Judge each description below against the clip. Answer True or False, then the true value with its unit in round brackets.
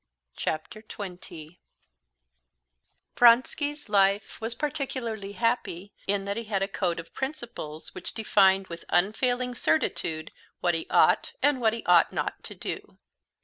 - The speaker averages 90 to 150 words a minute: True (135 wpm)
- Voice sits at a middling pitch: False (205 Hz)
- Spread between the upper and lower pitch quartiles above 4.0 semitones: True (5.1 semitones)